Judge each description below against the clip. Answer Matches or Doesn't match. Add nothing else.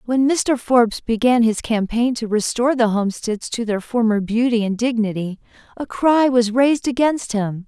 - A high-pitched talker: Matches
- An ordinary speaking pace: Matches